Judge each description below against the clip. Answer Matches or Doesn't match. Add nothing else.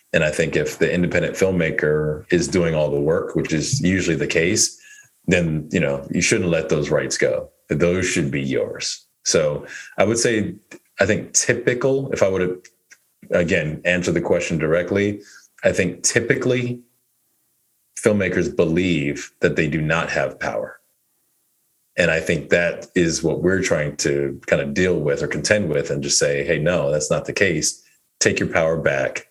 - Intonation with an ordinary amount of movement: Doesn't match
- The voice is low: Matches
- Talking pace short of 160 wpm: Doesn't match